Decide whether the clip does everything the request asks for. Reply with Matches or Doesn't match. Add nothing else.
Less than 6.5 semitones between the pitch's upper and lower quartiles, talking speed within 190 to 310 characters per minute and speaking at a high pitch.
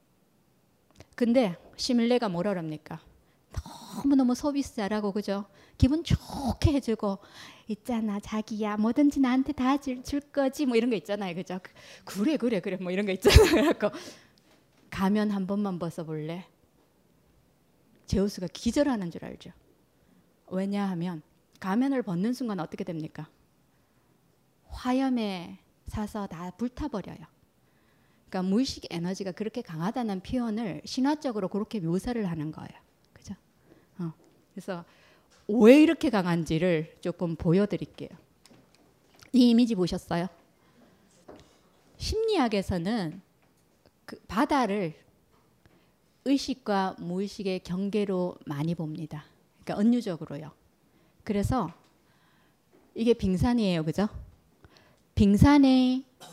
Matches